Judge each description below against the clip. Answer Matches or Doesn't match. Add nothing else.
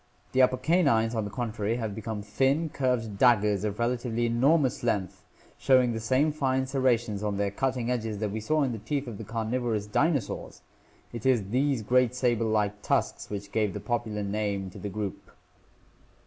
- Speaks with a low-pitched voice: Matches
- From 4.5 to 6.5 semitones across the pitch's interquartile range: Doesn't match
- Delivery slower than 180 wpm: Doesn't match